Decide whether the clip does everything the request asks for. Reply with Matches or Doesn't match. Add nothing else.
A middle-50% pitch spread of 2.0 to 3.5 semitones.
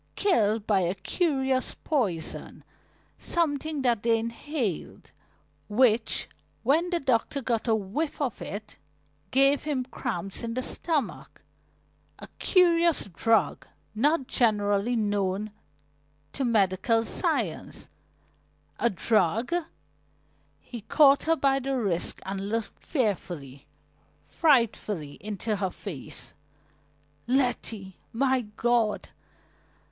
Doesn't match